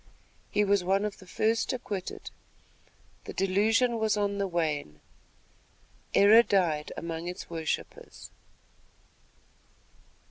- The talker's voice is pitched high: Yes, high, 195 Hz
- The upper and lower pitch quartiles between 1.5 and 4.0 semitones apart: Yes, average, 3.6 semitones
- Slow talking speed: Yes, slow, 105 wpm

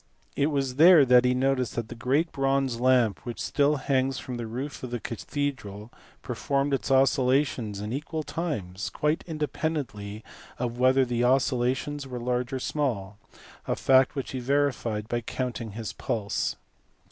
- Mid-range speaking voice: No, low, 130 Hz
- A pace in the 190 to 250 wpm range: No, average, 160 wpm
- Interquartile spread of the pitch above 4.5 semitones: No, average, 2.9 semitones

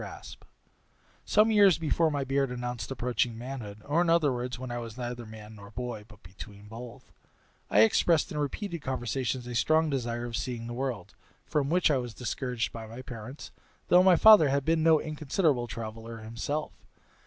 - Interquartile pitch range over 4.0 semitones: Yes, average, 4.5 semitones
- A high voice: No, low, 125 Hz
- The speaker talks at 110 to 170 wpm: No, average, 180 wpm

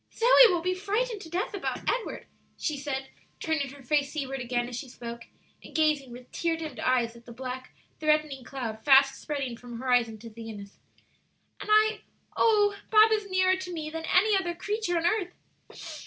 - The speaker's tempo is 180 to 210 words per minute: Yes, average, 185 wpm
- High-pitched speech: Yes, very high, 305 Hz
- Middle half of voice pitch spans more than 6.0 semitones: Yes, wide, 6.9 semitones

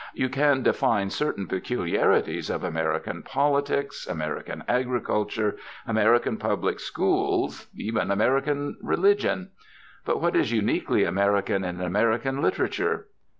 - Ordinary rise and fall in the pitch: No, wide, 6.0 semitones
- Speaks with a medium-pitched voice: No, low, 115 Hz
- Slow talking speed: Yes, slow, 110 wpm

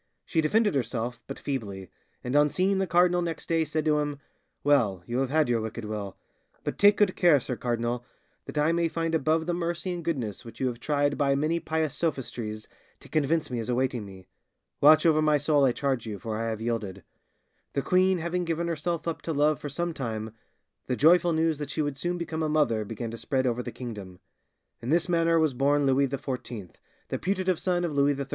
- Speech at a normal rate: No, fast, 215 wpm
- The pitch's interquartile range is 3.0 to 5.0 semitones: No, wide, 5.4 semitones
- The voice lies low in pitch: No, medium, 145 Hz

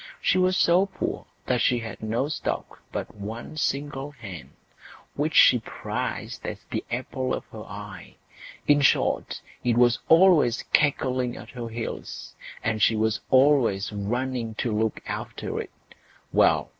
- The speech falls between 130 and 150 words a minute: Yes, average, 145 wpm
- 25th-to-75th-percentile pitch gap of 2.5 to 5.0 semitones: Yes, average, 4.4 semitones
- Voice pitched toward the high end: No, low, 125 Hz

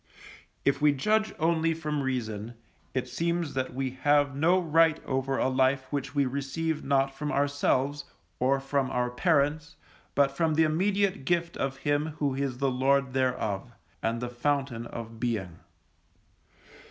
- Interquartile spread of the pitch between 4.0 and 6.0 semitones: No, average, 2.8 semitones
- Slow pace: No, average, 155 wpm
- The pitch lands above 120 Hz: Yes, medium, 140 Hz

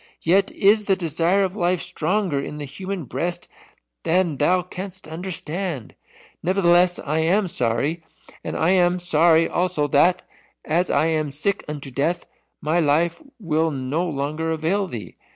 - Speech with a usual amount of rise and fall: Yes, average, 3.3 semitones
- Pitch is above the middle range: No, medium, 170 Hz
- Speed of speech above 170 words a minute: No, average, 150 wpm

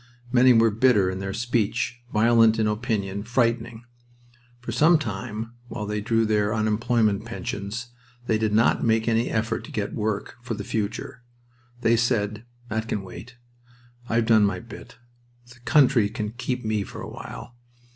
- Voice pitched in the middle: No, low, 110 Hz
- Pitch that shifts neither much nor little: No, narrow, 2.0 semitones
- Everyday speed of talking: Yes, average, 160 wpm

